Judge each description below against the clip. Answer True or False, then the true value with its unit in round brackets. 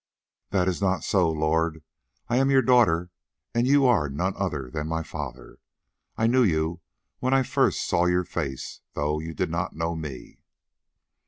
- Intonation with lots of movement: True (6.1 semitones)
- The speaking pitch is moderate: False (85 Hz)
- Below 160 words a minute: False (170 wpm)